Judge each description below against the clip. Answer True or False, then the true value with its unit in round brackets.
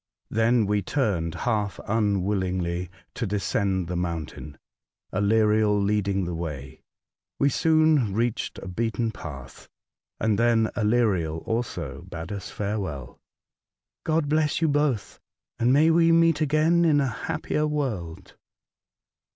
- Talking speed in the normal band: False (125 wpm)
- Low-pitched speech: True (105 Hz)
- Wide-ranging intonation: True (7.0 semitones)